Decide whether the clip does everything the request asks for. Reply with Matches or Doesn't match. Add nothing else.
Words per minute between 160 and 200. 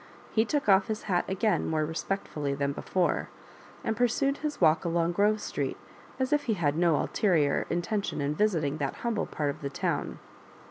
Matches